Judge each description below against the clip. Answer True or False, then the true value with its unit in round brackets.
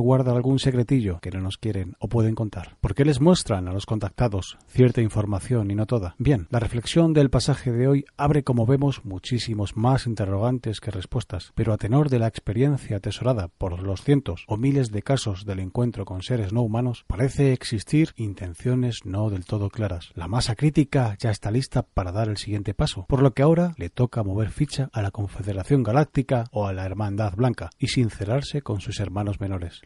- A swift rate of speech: True (195 wpm)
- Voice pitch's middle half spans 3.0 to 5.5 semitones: True (4.5 semitones)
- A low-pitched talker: True (115 Hz)